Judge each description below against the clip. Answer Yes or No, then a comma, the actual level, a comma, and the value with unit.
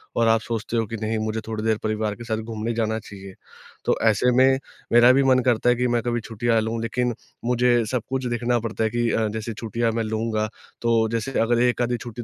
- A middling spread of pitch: No, narrow, 1.5 semitones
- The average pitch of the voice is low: Yes, low, 115 Hz